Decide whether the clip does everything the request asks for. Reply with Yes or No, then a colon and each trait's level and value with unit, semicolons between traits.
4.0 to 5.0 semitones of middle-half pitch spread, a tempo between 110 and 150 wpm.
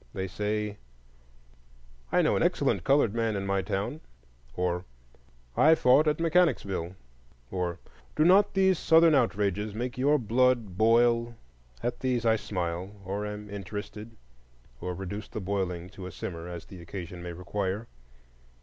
Yes: average, 4.6 semitones; average, 145 wpm